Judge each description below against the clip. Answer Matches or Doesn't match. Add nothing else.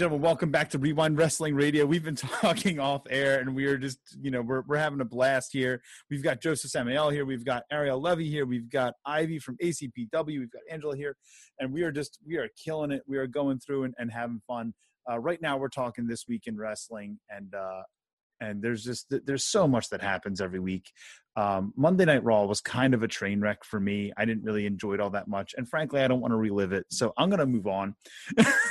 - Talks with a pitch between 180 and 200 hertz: Doesn't match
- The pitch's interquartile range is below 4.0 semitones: Doesn't match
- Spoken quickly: Matches